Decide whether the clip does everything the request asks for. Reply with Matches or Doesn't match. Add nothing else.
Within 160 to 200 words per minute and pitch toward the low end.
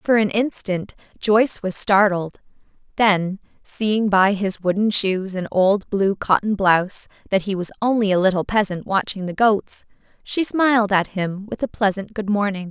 Doesn't match